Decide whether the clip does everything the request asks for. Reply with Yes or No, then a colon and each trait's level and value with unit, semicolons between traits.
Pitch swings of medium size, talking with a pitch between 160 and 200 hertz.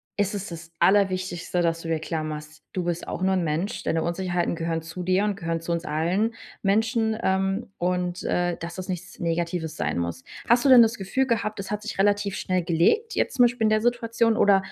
Yes: average, 4.0 semitones; medium, 185 Hz